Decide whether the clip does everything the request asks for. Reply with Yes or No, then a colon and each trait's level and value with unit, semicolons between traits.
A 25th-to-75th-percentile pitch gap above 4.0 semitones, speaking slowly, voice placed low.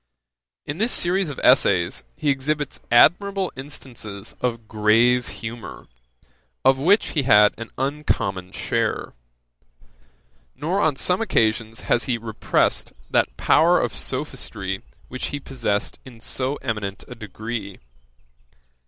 Yes: average, 5.2 semitones; slow, 120 wpm; low, 125 Hz